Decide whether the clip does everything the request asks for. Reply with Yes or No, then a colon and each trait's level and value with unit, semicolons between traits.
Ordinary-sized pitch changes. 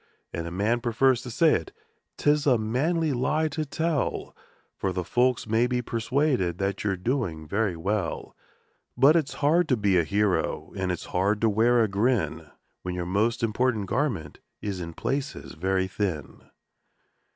No: wide, 5.7 semitones